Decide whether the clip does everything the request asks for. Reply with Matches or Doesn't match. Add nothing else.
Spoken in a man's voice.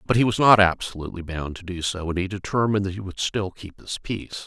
Matches